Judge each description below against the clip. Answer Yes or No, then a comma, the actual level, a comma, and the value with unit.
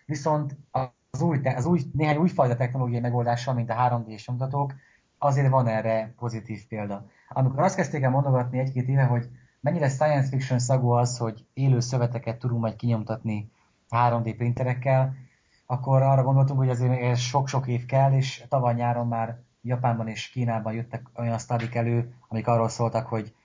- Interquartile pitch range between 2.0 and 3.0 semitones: Yes, narrow, 2.4 semitones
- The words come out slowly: No, fast, 160 wpm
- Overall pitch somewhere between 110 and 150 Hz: Yes, low, 125 Hz